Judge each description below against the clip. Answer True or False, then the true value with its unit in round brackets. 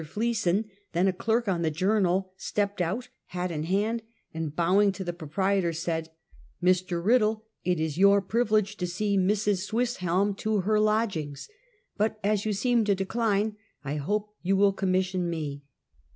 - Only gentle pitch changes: False (3.3 semitones)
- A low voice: False (195 Hz)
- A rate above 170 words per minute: False (165 wpm)